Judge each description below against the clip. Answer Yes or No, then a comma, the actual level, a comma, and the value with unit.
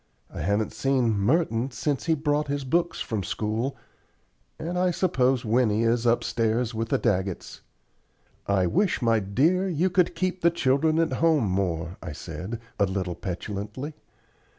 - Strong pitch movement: Yes, wide, 7.4 semitones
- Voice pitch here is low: Yes, low, 120 Hz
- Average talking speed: Yes, average, 150 wpm